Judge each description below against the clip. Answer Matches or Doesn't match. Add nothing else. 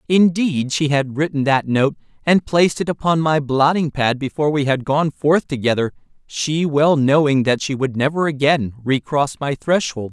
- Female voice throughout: Doesn't match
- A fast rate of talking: Doesn't match